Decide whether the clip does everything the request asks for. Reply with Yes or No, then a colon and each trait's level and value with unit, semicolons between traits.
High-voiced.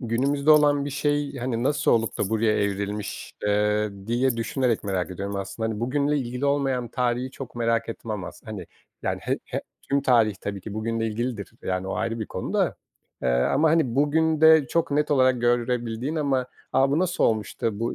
No: low, 120 Hz